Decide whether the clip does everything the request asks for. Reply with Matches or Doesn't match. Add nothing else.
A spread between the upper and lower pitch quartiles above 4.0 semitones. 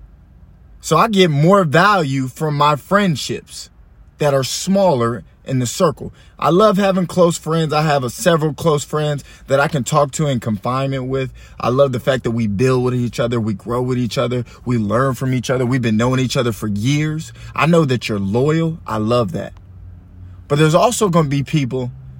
Matches